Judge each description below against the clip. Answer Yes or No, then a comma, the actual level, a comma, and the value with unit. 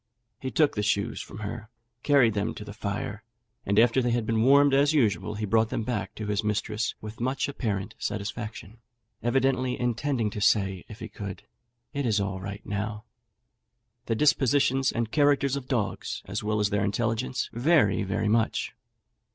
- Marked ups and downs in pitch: No, average, 3.7 semitones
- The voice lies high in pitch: No, low, 110 Hz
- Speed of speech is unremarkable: Yes, average, 175 wpm